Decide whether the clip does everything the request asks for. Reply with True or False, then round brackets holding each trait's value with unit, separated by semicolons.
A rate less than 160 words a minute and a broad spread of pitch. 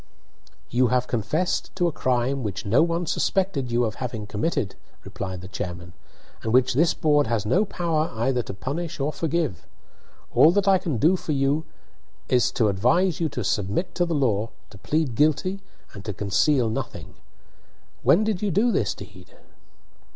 False (175 wpm; 7.3 semitones)